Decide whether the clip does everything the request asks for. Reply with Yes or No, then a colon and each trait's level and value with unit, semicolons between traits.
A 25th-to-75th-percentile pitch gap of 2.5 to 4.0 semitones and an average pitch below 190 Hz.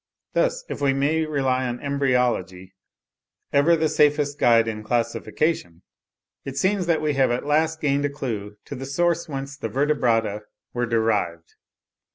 No: average, 4.6 semitones; low, 135 Hz